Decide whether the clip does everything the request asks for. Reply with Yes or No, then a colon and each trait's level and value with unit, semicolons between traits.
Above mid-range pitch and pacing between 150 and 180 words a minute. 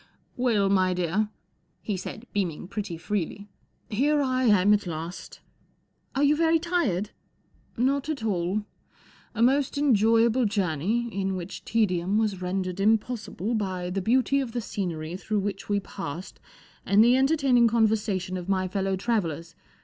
Yes: high, 205 Hz; average, 160 wpm